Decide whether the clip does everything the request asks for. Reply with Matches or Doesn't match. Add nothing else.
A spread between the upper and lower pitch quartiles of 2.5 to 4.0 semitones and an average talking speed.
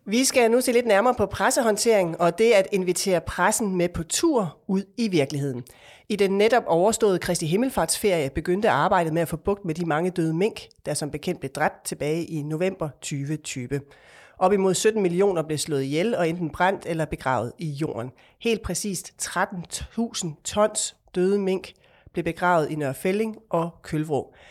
Doesn't match